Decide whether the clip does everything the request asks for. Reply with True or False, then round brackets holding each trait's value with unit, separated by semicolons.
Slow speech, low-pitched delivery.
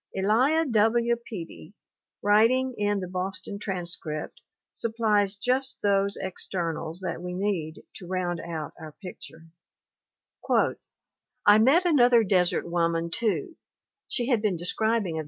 False (120 wpm; 200 Hz)